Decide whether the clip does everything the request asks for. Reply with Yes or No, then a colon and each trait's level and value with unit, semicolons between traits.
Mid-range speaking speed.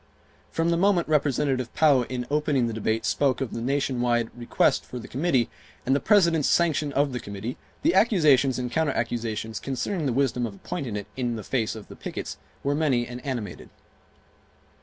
Yes: average, 185 wpm